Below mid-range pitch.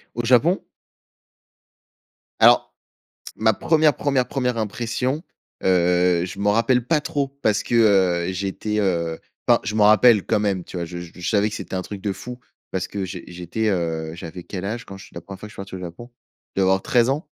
Yes: low, 100 Hz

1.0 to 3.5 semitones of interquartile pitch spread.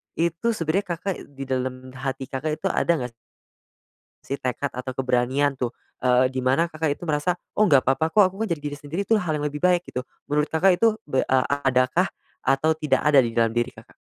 No: average, 4.4 semitones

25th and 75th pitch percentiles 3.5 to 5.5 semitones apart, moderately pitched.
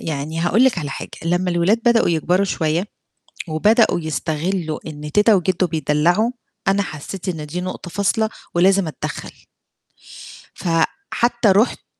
Yes: average, 4.1 semitones; medium, 175 Hz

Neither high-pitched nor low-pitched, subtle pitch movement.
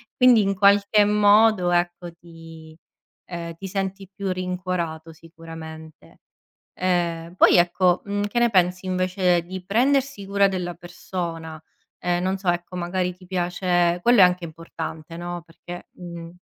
Yes: medium, 180 Hz; narrow, 2.3 semitones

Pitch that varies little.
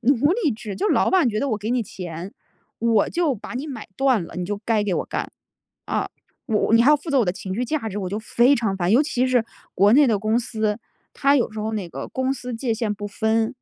No: average, 4.0 semitones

